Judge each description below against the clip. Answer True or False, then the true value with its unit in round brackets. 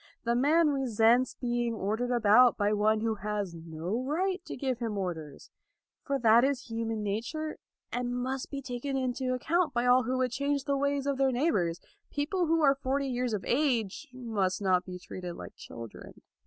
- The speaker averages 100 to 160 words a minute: False (180 wpm)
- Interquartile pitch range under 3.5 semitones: False (4.5 semitones)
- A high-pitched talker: True (245 Hz)